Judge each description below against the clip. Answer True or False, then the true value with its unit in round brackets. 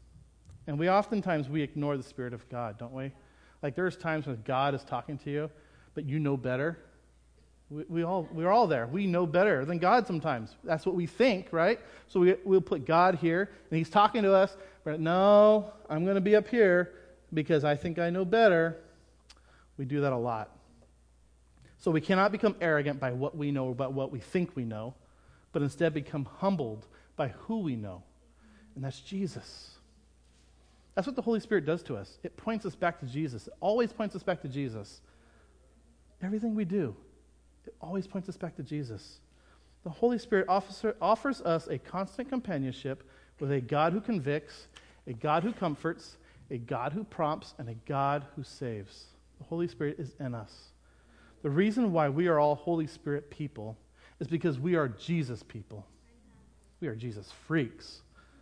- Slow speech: False (185 wpm)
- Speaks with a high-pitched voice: False (150 Hz)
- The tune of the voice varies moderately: False (7.5 semitones)